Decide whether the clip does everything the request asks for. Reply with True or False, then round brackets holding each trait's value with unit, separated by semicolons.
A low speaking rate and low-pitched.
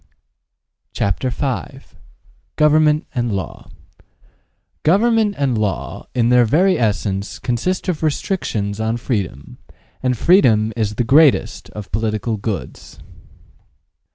True (105 wpm; 120 Hz)